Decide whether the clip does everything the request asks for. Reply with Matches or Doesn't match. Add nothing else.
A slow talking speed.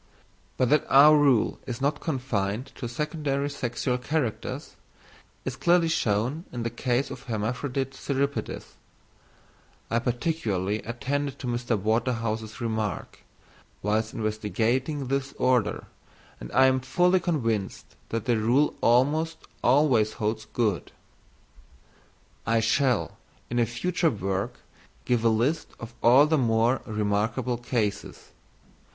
Matches